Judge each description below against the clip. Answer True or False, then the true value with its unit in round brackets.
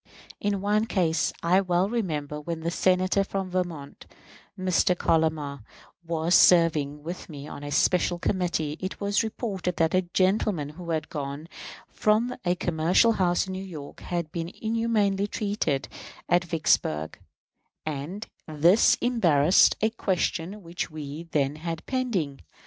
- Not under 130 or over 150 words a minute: True (140 wpm)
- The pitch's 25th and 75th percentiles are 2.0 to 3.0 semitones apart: False (3.8 semitones)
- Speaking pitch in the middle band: True (175 Hz)